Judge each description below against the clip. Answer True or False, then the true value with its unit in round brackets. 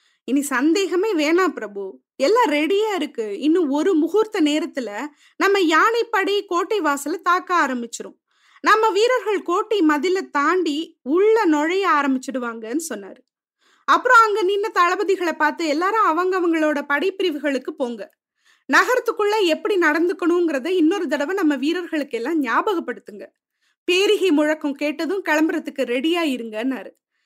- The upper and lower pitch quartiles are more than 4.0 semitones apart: True (4.6 semitones)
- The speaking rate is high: False (110 wpm)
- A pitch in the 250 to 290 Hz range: False (330 Hz)